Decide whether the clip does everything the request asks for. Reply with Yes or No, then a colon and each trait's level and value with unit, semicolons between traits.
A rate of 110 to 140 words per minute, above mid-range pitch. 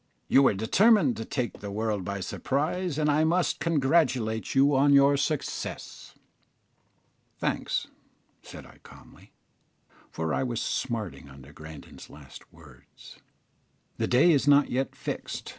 No: slow, 135 wpm; low, 130 Hz